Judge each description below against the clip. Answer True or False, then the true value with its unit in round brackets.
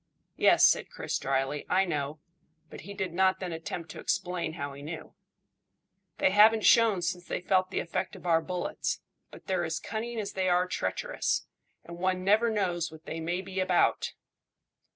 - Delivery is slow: False (180 wpm)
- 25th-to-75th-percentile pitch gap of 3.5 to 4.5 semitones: False (2.7 semitones)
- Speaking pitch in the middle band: True (180 Hz)